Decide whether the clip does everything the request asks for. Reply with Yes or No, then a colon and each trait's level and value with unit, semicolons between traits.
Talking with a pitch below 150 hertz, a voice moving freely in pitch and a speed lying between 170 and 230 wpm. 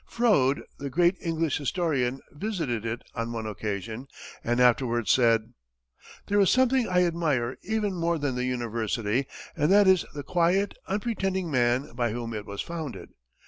No: medium, 140 Hz; wide, 7.2 semitones; average, 155 wpm